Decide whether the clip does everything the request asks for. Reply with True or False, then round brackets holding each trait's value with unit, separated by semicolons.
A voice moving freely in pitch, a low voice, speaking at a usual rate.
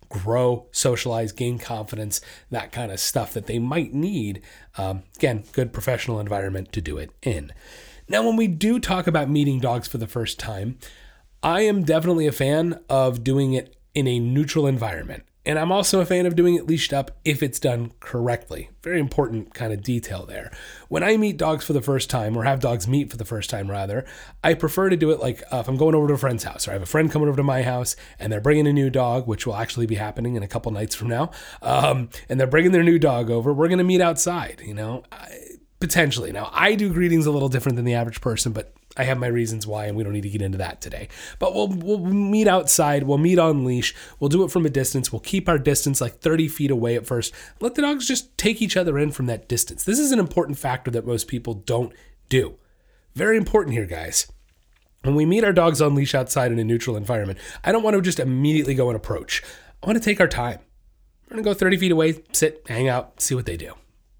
False (5.9 semitones; 130 Hz; 240 wpm)